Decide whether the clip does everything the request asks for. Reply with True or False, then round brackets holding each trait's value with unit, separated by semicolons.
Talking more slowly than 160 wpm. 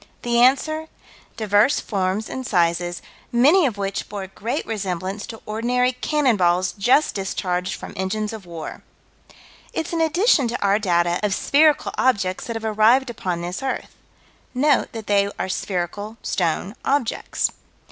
True (150 wpm)